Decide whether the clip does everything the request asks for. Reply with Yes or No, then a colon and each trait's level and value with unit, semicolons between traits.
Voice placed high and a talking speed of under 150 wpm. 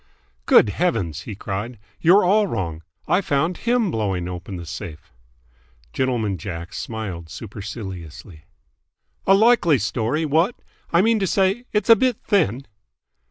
No: low, 120 Hz; slow, 135 wpm